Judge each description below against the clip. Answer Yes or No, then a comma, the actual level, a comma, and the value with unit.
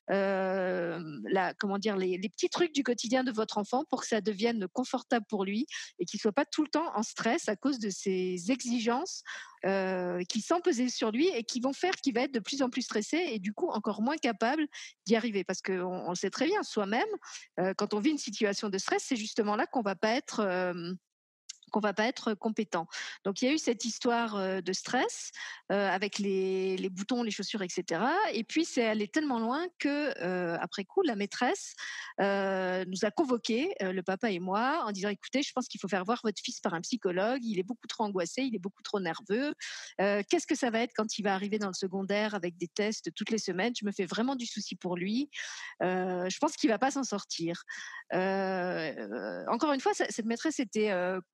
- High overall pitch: Yes, high, 215 Hz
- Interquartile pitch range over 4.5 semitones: Yes, average, 5.0 semitones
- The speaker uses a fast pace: Yes, fast, 225 wpm